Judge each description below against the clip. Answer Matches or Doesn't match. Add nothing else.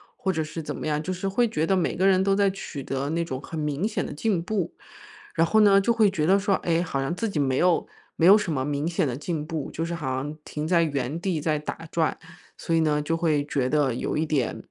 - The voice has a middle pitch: Matches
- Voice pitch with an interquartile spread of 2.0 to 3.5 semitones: Doesn't match